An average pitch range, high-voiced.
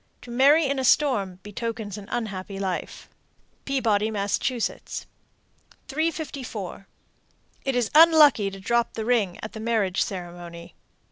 Yes: average, 5.0 semitones; high, 220 Hz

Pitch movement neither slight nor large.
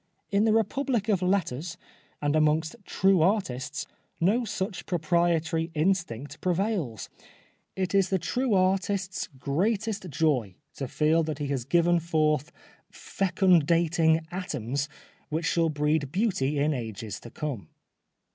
Yes: average, 4.5 semitones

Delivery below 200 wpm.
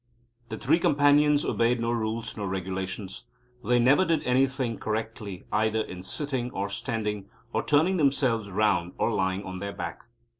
Yes: average, 155 wpm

